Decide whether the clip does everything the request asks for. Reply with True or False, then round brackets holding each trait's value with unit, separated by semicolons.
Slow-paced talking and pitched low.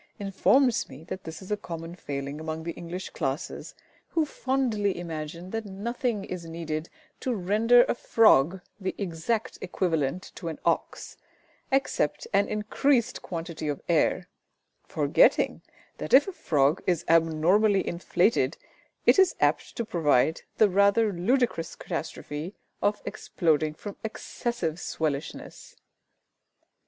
False (125 wpm; 180 Hz)